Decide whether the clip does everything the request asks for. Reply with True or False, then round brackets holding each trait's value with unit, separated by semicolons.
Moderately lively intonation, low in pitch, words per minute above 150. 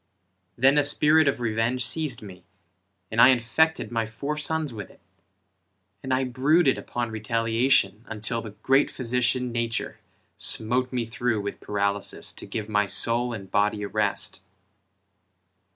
False (3.2 semitones; 120 Hz; 145 wpm)